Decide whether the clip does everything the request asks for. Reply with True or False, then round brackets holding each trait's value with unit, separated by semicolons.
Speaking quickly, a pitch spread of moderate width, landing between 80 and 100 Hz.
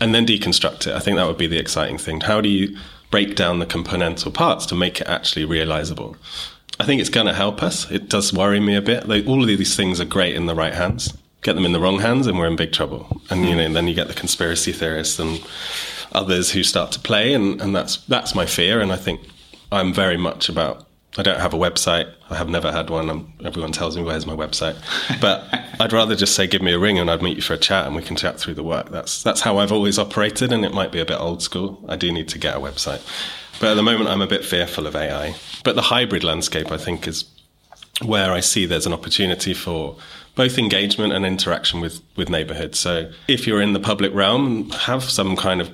True (250 wpm; 3.6 semitones; 90 Hz)